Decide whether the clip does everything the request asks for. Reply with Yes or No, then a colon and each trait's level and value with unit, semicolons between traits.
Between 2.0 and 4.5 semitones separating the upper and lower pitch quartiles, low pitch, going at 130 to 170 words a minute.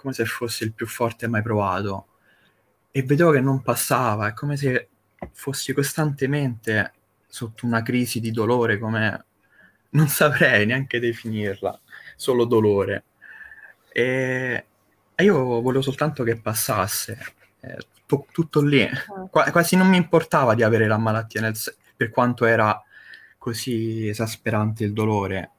Yes: average, 3.6 semitones; low, 115 Hz; average, 140 wpm